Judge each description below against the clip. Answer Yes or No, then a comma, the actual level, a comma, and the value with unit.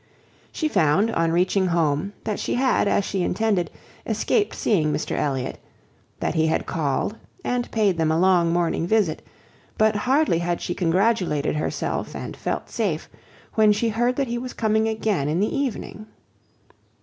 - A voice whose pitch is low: No, high, 195 Hz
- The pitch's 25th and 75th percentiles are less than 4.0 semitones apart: No, average, 5.1 semitones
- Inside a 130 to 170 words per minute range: Yes, average, 160 wpm